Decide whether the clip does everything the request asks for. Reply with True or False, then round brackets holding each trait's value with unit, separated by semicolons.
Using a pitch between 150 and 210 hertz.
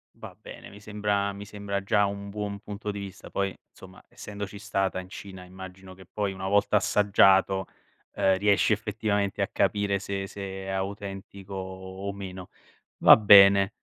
False (100 Hz)